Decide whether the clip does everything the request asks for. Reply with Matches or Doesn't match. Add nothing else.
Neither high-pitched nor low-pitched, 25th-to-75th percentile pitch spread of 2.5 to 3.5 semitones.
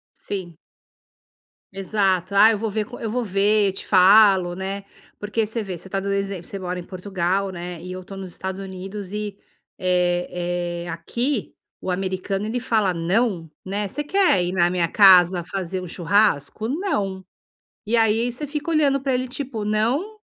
Doesn't match